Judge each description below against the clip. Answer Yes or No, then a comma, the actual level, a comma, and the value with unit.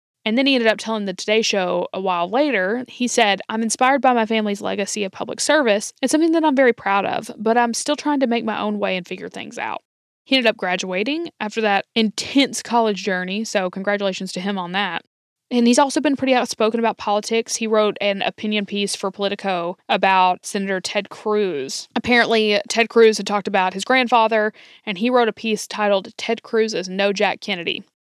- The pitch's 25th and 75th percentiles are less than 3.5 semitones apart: Yes, average, 2.9 semitones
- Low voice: No, high, 215 Hz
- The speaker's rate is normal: No, fast, 210 wpm